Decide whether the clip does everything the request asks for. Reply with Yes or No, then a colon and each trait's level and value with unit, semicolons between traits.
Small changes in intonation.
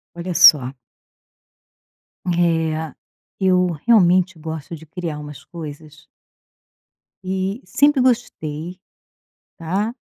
No: average, 3.2 semitones